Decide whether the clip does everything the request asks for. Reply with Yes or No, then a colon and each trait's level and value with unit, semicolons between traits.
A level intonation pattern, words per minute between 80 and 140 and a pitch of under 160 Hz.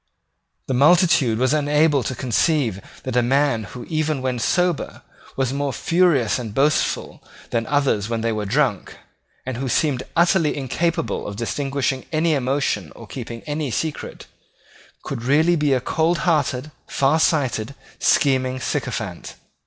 No: average, 3.8 semitones; slow, 135 wpm; medium, 140 Hz